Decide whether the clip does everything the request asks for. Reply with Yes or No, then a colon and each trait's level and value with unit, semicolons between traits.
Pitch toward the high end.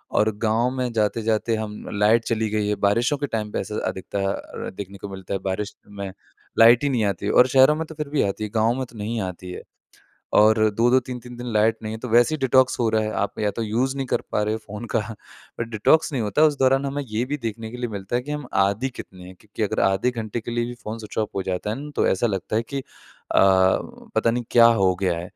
No: low, 110 Hz